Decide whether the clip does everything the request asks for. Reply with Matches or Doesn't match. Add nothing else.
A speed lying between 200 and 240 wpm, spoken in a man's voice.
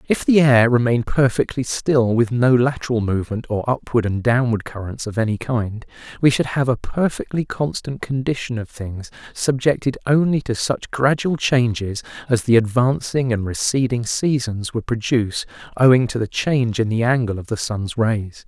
Doesn't match